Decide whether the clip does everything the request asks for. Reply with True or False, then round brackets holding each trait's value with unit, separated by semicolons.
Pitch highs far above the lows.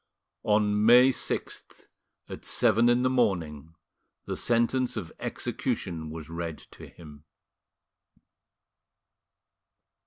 True (6.7 semitones)